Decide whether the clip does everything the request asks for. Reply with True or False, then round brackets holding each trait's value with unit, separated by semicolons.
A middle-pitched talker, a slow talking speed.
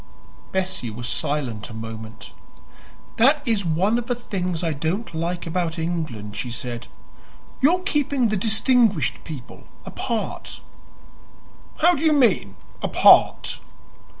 True (175 Hz; 125 wpm)